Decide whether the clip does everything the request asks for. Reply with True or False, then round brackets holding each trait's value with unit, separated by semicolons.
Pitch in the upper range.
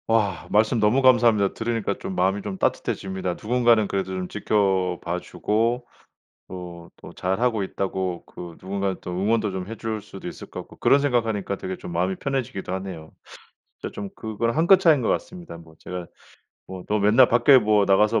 False (105 Hz)